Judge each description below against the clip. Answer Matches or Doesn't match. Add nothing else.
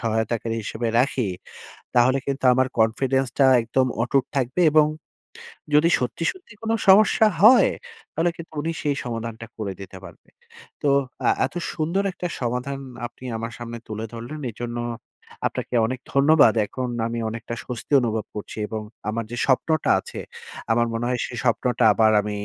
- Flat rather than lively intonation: Doesn't match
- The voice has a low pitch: Matches